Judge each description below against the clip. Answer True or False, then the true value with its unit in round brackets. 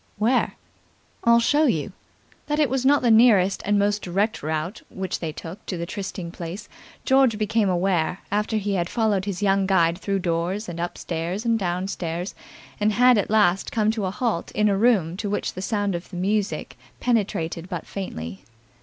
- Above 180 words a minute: True (190 wpm)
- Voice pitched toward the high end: True (195 Hz)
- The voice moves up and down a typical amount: True (3.7 semitones)